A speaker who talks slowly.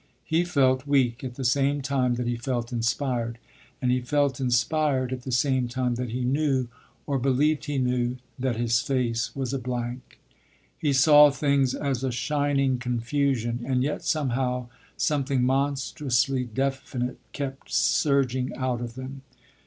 No: average, 155 wpm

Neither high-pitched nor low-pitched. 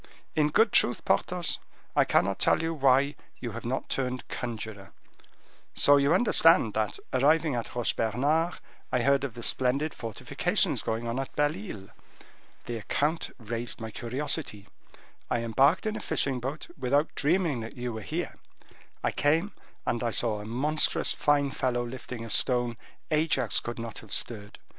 No: low, 125 Hz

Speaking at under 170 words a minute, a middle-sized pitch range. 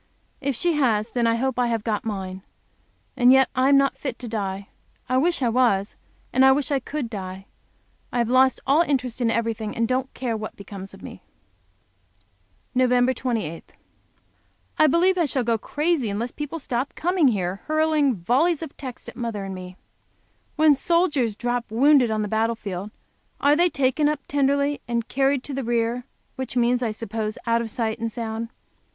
No: average, 190 wpm; average, 3.7 semitones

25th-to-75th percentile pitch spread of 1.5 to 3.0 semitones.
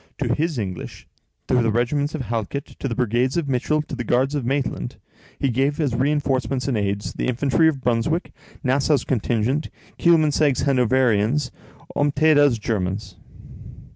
No: average, 3.7 semitones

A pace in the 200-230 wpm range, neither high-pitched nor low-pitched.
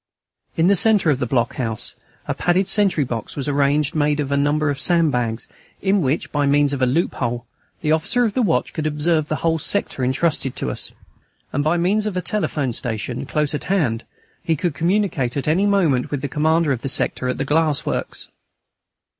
Yes: fast, 205 wpm; medium, 150 Hz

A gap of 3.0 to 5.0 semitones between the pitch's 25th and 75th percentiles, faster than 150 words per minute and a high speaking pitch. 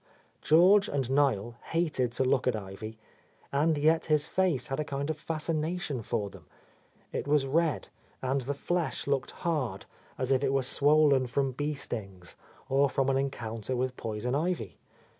No: average, 3.4 semitones; average, 170 wpm; medium, 140 Hz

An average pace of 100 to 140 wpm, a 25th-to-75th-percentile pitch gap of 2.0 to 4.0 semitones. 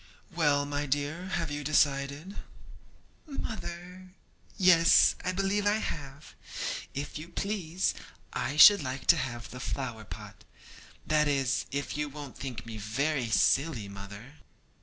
No: slow, 135 wpm; average, 4.4 semitones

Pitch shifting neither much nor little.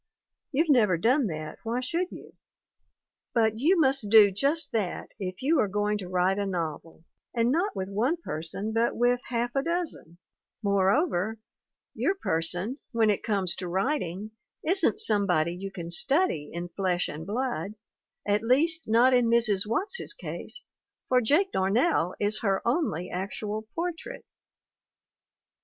No: wide, 6.3 semitones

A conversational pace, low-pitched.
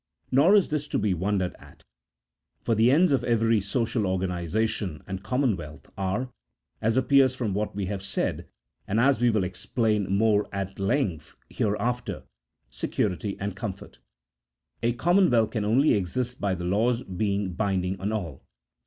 Yes: average, 160 wpm; low, 105 Hz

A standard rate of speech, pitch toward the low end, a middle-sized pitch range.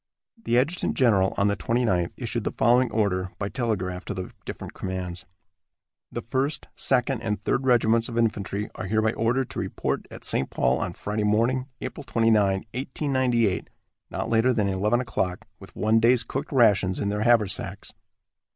Yes: average, 165 wpm; low, 110 Hz; average, 3.6 semitones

